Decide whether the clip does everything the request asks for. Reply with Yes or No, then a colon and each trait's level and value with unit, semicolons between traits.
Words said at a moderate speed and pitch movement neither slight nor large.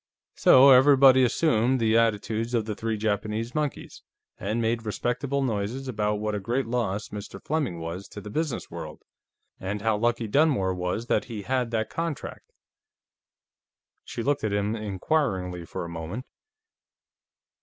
Yes: average, 150 wpm; average, 3.8 semitones